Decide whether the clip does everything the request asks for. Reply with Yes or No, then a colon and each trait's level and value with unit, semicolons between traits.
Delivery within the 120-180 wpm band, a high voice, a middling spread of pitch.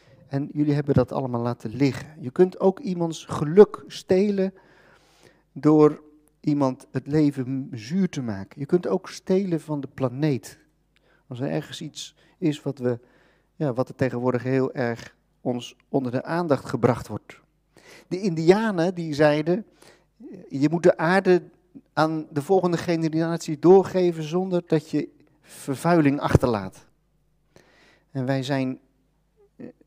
No: slow, 135 wpm; medium, 150 Hz; average, 4.3 semitones